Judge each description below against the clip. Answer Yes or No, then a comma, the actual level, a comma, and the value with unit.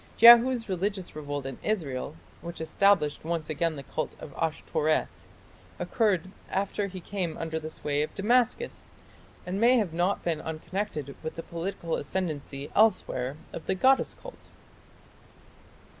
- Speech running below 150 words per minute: Yes, average, 140 wpm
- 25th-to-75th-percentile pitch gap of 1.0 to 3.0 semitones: No, average, 4.5 semitones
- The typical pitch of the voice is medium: Yes, medium, 170 Hz